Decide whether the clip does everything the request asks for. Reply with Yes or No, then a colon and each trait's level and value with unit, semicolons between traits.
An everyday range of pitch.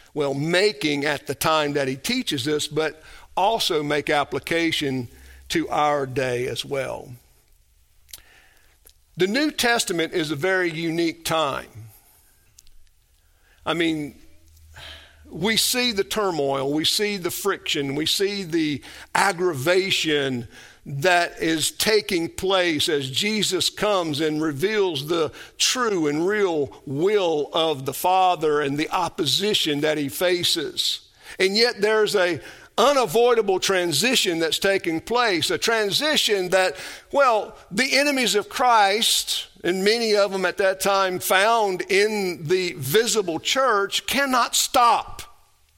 No: wide, 6.1 semitones